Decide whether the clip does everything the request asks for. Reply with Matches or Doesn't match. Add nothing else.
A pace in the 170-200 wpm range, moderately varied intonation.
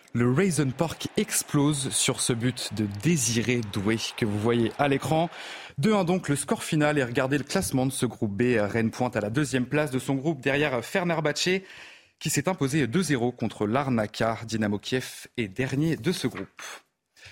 Matches